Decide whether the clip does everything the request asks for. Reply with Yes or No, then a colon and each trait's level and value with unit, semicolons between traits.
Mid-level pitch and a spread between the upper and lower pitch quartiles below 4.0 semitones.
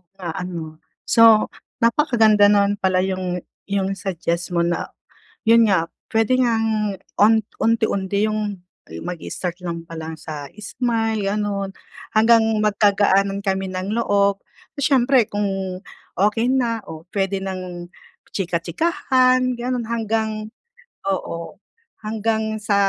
No: high, 205 Hz; average, 3.3 semitones